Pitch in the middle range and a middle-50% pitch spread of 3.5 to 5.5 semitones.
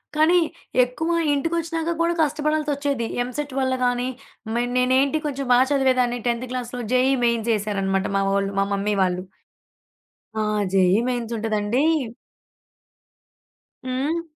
No: very high, 255 Hz; average, 4.2 semitones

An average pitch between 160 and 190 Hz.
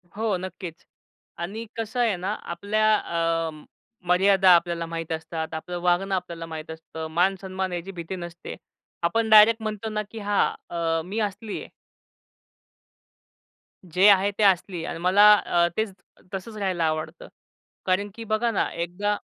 Yes: medium, 185 Hz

